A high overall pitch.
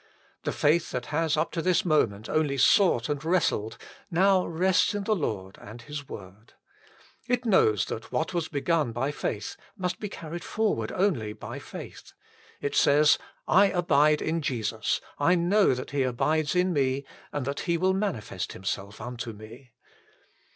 No: medium, 150 Hz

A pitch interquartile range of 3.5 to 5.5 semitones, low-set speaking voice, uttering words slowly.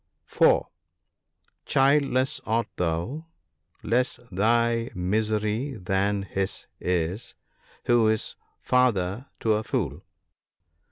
Yes: average, 4.2 semitones; low, 110 Hz; slow, 95 wpm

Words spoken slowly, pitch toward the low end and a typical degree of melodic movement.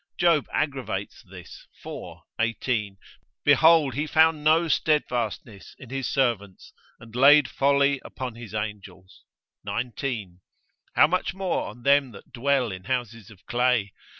Yes: slow, 130 wpm; low, 125 Hz; average, 4.3 semitones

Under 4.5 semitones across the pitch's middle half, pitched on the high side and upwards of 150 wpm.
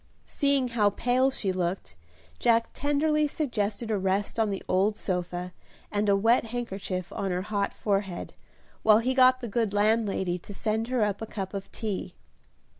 Yes: average, 3.7 semitones; high, 210 Hz; average, 170 wpm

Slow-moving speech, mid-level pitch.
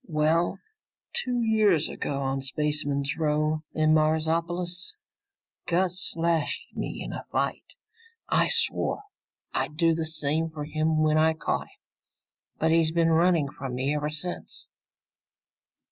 Yes: slow, 130 wpm; medium, 160 Hz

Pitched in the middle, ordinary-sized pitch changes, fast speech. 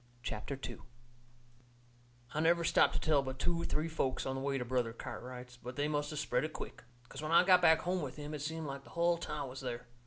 Yes: medium, 145 Hz; average, 3.7 semitones; fast, 240 wpm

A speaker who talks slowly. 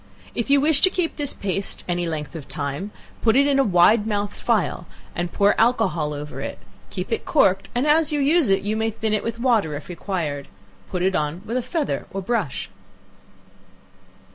No: average, 195 wpm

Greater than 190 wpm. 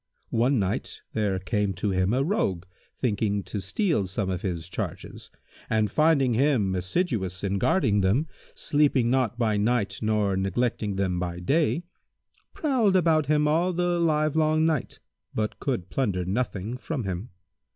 No: average, 150 wpm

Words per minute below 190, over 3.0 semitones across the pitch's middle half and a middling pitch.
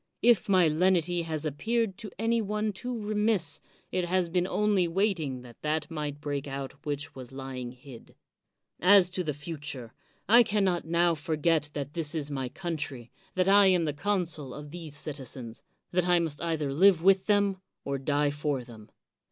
Yes: average, 180 wpm; average, 4.8 semitones; medium, 165 Hz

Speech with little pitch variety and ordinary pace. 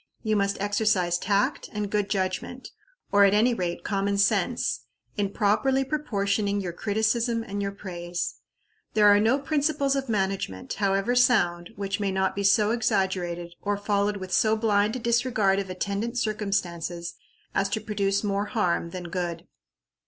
Yes: narrow, 2.3 semitones; average, 155 wpm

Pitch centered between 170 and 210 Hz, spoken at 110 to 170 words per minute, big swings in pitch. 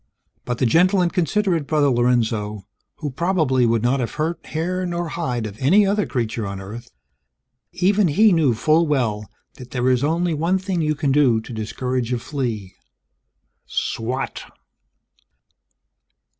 No: low, 135 Hz; average, 150 wpm; wide, 6.3 semitones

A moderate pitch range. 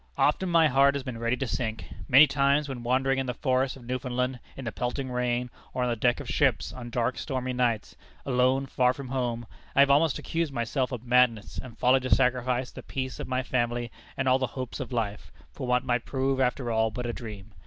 No: narrow, 1.7 semitones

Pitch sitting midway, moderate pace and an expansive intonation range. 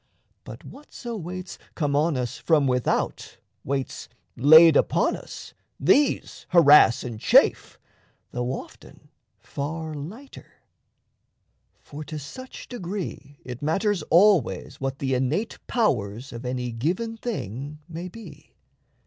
No: medium, 150 Hz; slow, 115 wpm; wide, 6.1 semitones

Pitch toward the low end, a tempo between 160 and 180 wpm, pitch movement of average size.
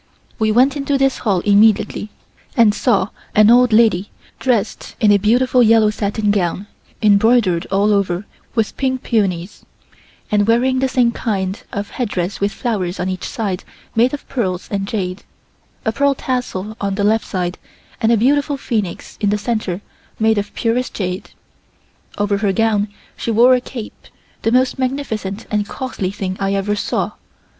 No: high, 215 Hz; average, 165 wpm; average, 3.4 semitones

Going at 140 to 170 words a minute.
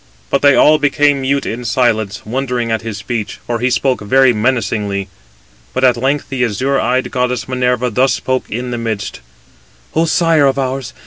No: average, 180 wpm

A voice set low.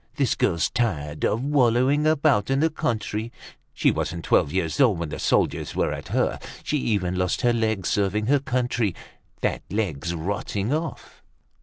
Yes: low, 110 Hz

